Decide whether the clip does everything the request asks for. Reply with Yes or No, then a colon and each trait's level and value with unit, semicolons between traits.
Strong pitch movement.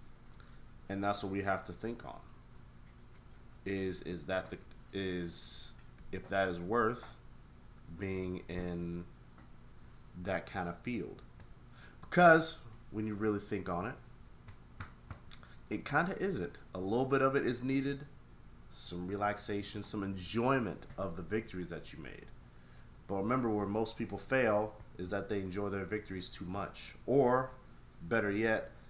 No: average, 3.8 semitones